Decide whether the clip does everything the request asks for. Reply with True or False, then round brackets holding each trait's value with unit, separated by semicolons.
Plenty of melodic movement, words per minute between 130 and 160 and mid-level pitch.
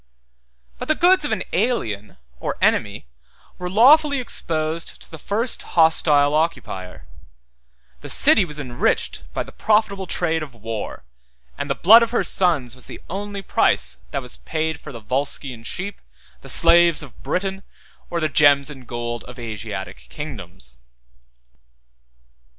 True (8.0 semitones; 145 wpm; 155 Hz)